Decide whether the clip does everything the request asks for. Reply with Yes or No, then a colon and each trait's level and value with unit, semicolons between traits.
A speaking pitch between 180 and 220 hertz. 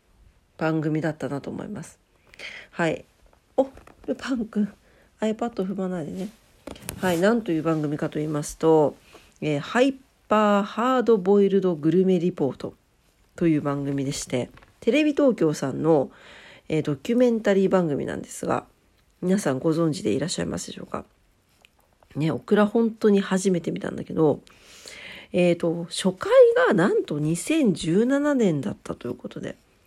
Yes: medium, 185 Hz